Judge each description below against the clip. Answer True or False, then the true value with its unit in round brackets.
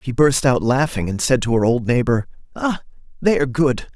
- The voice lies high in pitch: False (130 Hz)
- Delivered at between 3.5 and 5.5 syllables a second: True (5.4 syllables/s)